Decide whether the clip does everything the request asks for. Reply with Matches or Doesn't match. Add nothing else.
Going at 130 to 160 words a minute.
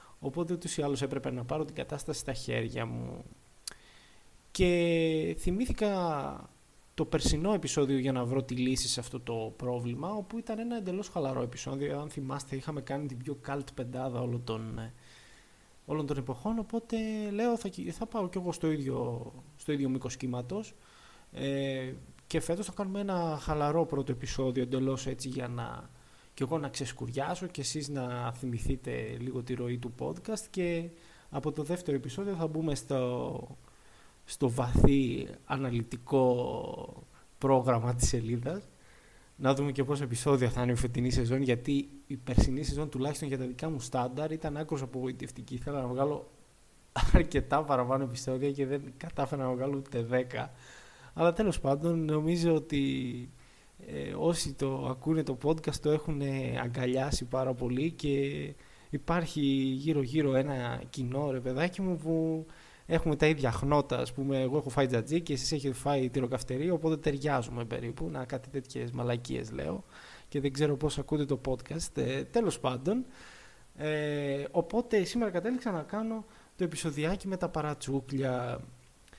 Matches